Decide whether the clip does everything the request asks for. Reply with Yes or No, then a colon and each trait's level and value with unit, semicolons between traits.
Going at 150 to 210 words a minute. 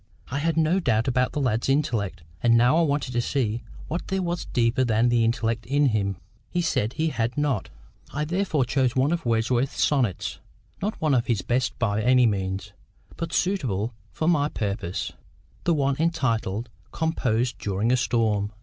Yes: average, 175 wpm